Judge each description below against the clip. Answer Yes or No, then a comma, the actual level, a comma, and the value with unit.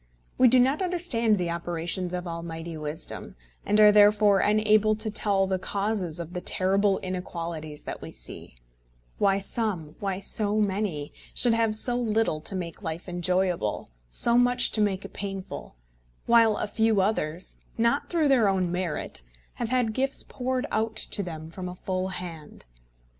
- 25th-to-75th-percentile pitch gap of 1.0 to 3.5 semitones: No, average, 3.9 semitones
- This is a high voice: Yes, high, 195 Hz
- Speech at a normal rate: Yes, average, 165 wpm